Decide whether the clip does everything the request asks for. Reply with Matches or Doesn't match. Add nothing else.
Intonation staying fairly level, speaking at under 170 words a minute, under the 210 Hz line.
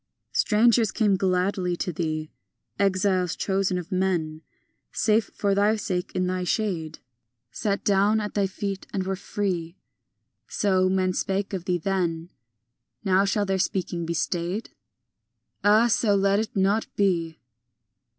Matches